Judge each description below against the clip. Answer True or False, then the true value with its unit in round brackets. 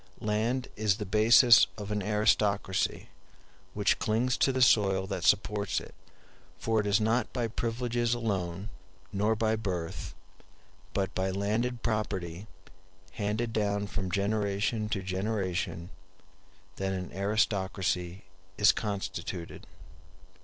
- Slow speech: True (115 wpm)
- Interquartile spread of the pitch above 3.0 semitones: False (2.5 semitones)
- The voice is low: True (105 Hz)